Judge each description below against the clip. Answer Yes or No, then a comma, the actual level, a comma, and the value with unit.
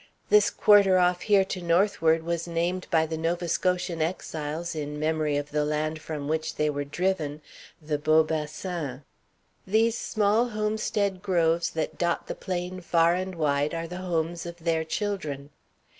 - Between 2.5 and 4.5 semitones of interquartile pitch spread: Yes, average, 3.0 semitones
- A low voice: No, medium, 170 Hz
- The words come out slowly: No, average, 160 wpm